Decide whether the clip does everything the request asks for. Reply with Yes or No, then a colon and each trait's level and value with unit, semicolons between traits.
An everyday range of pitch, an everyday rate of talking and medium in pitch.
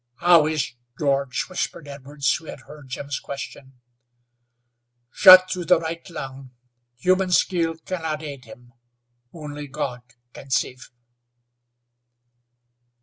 No: average, 3.6 semitones; slow, 115 wpm; medium, 150 Hz